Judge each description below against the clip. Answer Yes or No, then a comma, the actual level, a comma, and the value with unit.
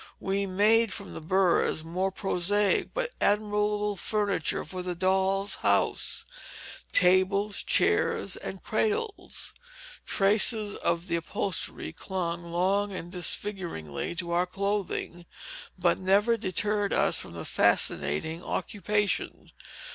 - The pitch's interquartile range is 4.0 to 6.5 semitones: No, average, 2.8 semitones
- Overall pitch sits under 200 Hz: Yes, high, 190 Hz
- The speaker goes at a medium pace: No, slow, 110 wpm